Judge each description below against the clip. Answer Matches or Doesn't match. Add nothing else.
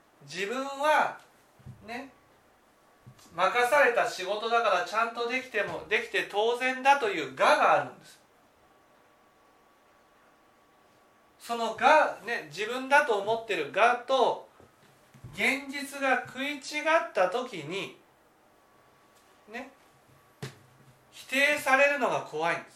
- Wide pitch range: Doesn't match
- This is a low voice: Doesn't match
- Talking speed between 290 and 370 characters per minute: Doesn't match